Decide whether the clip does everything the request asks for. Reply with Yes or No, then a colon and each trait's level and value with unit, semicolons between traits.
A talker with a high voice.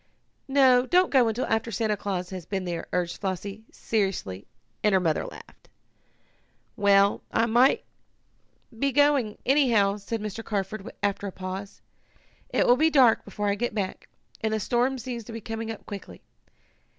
Yes: high, 215 Hz